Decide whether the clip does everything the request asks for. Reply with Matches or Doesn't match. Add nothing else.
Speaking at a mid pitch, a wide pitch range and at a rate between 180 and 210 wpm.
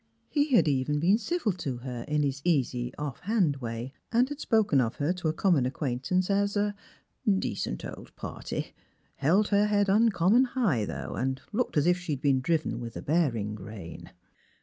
Matches